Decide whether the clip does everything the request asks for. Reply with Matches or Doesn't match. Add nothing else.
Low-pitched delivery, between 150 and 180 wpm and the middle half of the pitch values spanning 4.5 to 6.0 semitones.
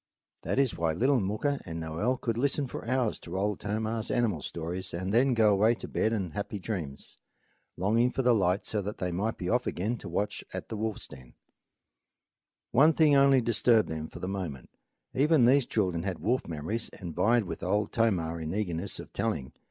Doesn't match